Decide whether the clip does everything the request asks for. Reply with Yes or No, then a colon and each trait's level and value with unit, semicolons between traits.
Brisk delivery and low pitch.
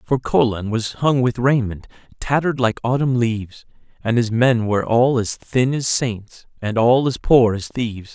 No: average, 185 wpm; low, 120 Hz